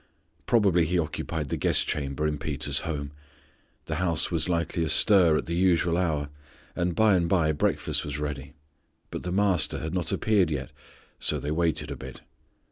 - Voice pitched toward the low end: Yes, very low, 80 Hz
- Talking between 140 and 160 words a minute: No, average, 175 wpm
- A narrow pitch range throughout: No, average, 3.1 semitones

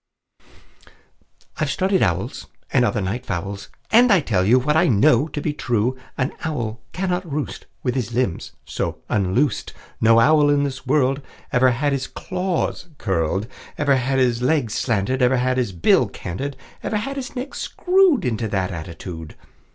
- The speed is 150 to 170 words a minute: Yes, average, 165 wpm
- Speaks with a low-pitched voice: Yes, low, 130 Hz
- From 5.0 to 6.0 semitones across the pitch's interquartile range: Yes, wide, 5.6 semitones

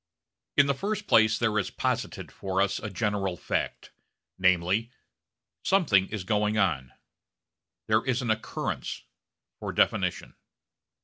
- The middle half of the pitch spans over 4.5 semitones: No, average, 3.4 semitones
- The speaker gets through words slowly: Yes, slow, 125 wpm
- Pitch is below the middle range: Yes, low, 105 Hz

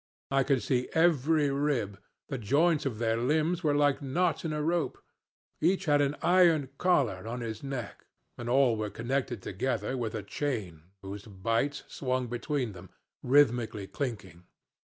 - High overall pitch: No, low, 130 Hz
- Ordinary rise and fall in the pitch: Yes, average, 4.6 semitones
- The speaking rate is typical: Yes, average, 155 wpm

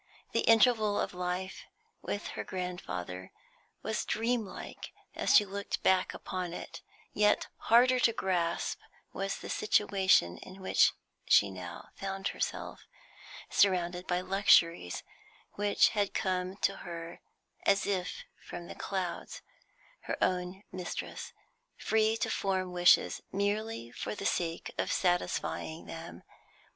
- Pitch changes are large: No, narrow, 2.5 semitones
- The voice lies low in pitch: No, medium, 185 Hz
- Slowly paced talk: Yes, slow, 125 wpm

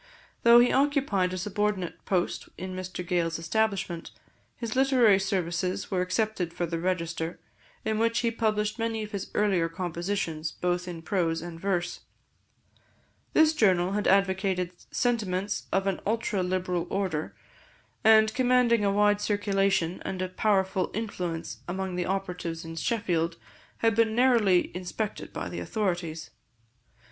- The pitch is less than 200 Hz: Yes, high, 190 Hz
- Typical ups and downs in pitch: Yes, average, 3.5 semitones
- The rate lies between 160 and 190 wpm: No, average, 140 wpm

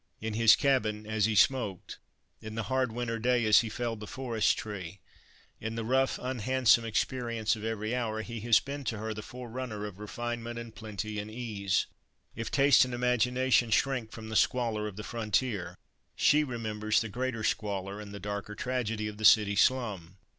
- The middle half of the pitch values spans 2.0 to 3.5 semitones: Yes, narrow, 2.5 semitones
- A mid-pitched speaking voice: No, low, 110 Hz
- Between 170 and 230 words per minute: Yes, average, 180 wpm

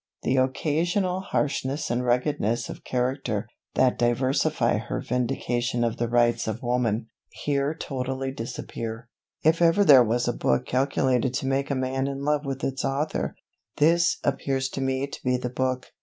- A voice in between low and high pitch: No, low, 130 Hz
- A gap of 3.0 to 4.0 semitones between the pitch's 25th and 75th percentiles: No, narrow, 2.5 semitones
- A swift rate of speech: No, average, 160 wpm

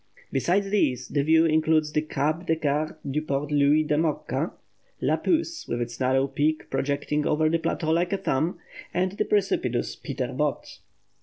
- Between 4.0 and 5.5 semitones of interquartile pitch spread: No, narrow, 2.5 semitones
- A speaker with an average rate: Yes, average, 170 wpm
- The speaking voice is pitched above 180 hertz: No, medium, 155 Hz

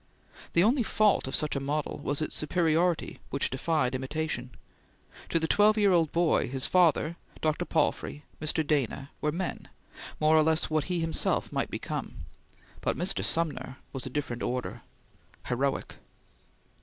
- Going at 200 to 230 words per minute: No, average, 155 wpm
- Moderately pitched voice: Yes, medium, 155 Hz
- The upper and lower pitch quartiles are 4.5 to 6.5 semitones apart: No, average, 3.5 semitones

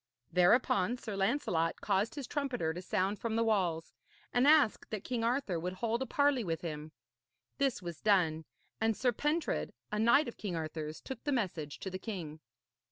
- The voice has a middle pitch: No, high, 210 Hz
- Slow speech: No, average, 180 wpm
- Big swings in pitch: Yes, wide, 6.2 semitones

